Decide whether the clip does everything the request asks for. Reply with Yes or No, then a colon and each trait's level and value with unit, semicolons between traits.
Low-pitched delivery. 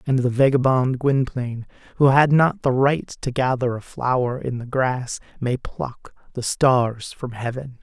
Yes: low, 130 Hz